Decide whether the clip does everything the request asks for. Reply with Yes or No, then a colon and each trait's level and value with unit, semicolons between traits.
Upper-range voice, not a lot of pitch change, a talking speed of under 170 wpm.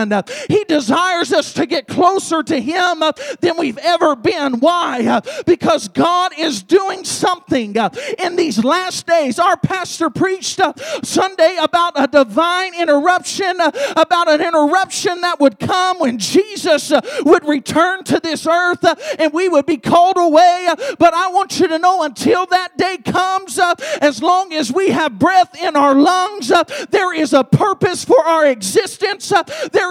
No: very high, 345 Hz; average, 3.2 semitones; average, 155 wpm